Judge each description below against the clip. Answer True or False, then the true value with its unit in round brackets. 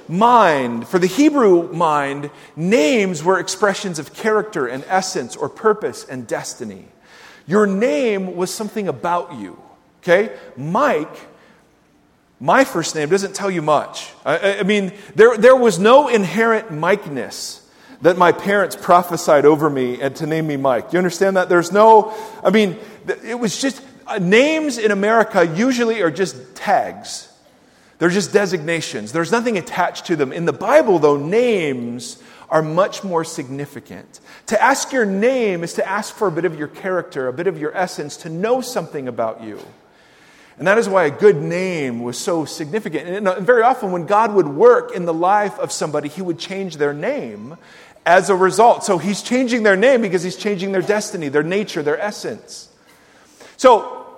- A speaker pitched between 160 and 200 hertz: True (190 Hz)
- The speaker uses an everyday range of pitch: True (5.0 semitones)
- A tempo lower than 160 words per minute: False (170 wpm)